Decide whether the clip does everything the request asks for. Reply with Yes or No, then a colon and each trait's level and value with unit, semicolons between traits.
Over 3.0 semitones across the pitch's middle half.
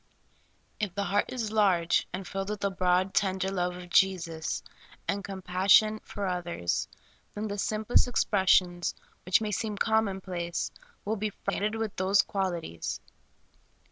No: narrow, 2.6 semitones